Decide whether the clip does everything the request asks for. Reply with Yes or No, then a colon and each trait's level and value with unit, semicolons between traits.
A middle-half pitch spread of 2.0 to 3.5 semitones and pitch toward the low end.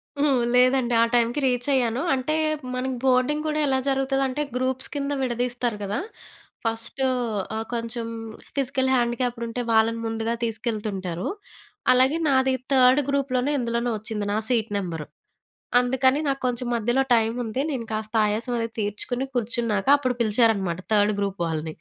No: average, 2.9 semitones; high, 240 Hz